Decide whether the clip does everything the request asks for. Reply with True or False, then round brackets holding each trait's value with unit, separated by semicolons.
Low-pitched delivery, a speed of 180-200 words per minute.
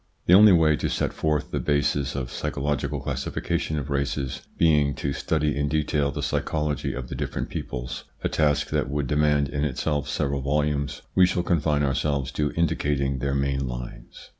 True (70 Hz; 185 wpm)